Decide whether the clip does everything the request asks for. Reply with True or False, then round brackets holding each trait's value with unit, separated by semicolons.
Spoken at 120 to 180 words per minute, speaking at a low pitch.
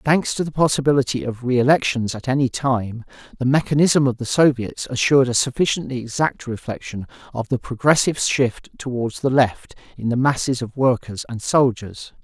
True (160 wpm; 130 Hz)